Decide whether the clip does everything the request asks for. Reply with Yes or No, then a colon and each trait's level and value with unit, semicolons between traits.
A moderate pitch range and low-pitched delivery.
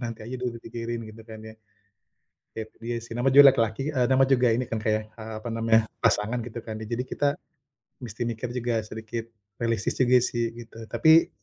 No: narrow, 1.7 semitones; low, 115 Hz